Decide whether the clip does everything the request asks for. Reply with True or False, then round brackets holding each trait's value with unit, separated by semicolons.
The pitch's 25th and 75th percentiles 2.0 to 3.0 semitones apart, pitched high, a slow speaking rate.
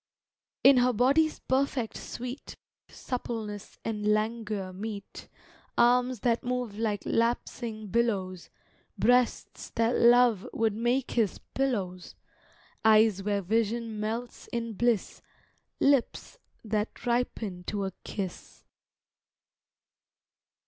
True (2.7 semitones; 230 Hz; 100 wpm)